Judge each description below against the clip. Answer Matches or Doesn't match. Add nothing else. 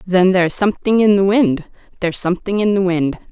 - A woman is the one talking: Matches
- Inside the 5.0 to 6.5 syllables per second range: Matches